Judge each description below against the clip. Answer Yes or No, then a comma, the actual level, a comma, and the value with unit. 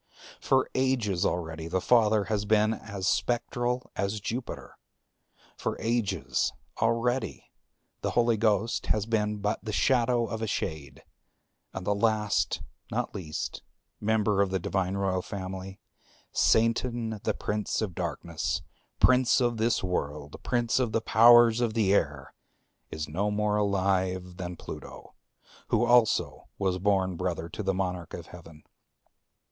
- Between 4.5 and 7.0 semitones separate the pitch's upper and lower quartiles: No, average, 3.8 semitones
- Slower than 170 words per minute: Yes, average, 140 wpm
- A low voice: Yes, low, 105 Hz